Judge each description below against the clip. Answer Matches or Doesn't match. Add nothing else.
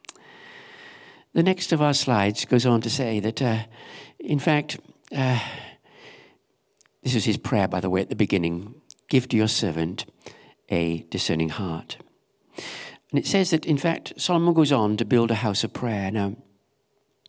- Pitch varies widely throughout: Matches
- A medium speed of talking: Matches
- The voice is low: Matches